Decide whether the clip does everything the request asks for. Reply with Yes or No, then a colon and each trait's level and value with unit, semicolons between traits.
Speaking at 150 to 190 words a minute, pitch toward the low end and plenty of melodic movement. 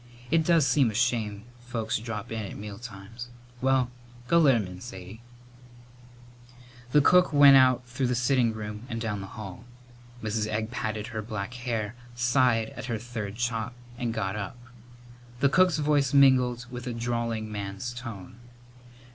No: average, 160 wpm; low, 120 Hz; average, 2.8 semitones